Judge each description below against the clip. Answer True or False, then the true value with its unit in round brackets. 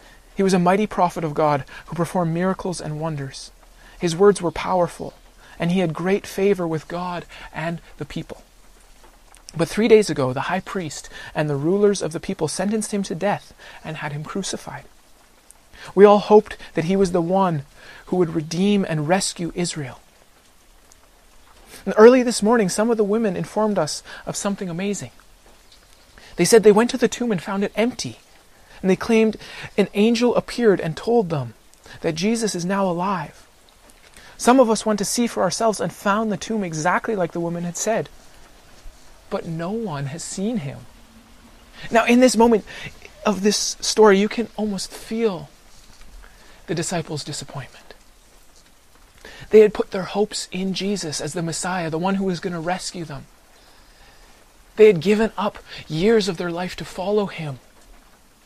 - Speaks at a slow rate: False (170 wpm)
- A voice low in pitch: False (190 Hz)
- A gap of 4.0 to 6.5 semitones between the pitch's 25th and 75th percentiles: True (4.3 semitones)